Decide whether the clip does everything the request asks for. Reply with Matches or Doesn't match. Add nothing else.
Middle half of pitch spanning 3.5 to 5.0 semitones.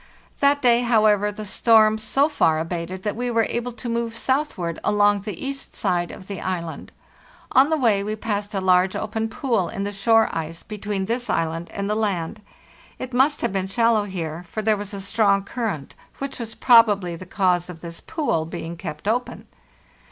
Matches